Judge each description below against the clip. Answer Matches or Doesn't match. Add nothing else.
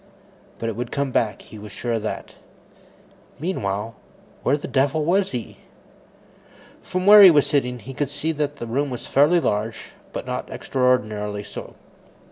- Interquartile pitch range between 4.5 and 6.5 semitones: Matches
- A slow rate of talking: Doesn't match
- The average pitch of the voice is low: Matches